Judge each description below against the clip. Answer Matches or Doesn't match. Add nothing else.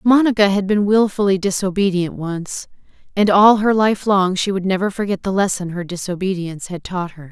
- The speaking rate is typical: Matches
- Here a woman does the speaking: Matches